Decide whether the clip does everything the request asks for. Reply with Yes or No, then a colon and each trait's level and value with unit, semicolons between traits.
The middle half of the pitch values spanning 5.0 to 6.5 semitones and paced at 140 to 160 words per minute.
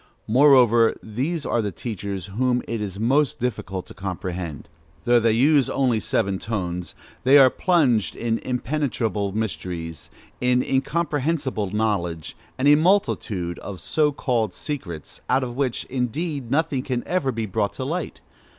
Yes: wide, 5.5 semitones; average, 145 wpm